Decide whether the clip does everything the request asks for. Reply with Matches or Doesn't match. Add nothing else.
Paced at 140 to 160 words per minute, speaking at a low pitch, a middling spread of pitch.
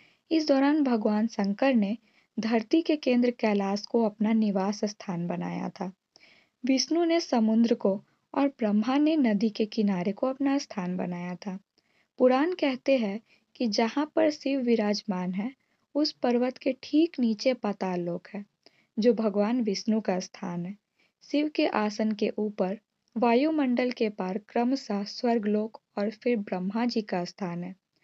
Doesn't match